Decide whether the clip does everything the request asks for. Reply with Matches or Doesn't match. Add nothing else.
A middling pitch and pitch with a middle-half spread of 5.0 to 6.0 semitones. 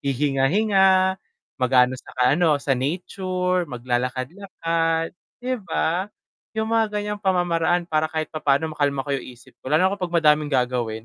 Matches